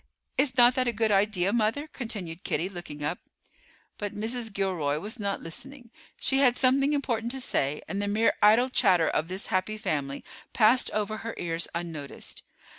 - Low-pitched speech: No, high, 210 Hz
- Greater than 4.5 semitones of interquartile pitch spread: Yes, wide, 5.6 semitones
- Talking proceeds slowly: No, average, 175 wpm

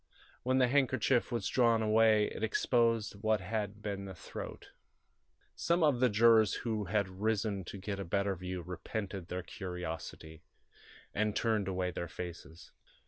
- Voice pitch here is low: Yes, low, 105 Hz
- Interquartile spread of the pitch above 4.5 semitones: No, average, 3.4 semitones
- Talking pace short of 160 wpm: Yes, average, 150 wpm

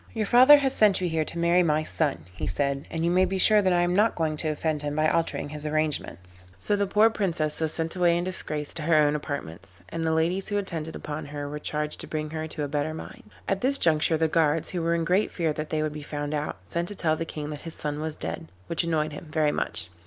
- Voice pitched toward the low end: No, medium, 155 Hz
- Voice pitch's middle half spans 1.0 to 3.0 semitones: Yes, narrow, 2.6 semitones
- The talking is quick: Yes, fast, 265 wpm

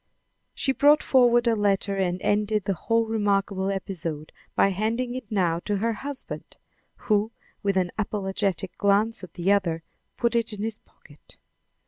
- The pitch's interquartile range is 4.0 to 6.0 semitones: No, average, 2.9 semitones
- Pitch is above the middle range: Yes, high, 205 Hz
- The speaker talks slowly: No, average, 155 wpm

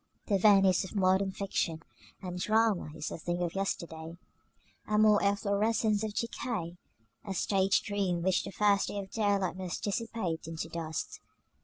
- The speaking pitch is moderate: No, high, 195 Hz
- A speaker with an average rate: Yes, average, 155 wpm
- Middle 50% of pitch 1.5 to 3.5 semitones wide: Yes, average, 2.9 semitones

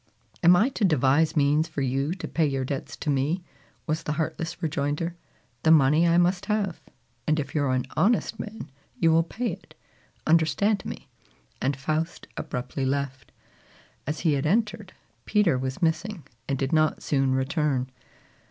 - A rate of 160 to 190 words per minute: Yes, average, 165 wpm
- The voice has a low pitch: No, medium, 155 Hz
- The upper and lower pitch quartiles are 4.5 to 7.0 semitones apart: No, average, 3.9 semitones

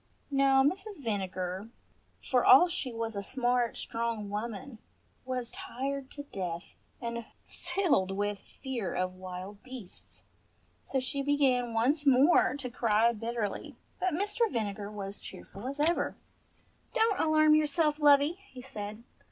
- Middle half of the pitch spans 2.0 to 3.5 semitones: No, wide, 5.6 semitones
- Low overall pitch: No, very high, 250 Hz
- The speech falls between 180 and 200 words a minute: No, slow, 135 wpm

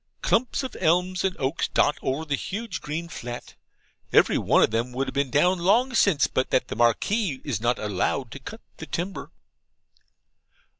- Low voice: No, medium, 150 Hz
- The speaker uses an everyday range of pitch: No, wide, 6.7 semitones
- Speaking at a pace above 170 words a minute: Yes, average, 180 wpm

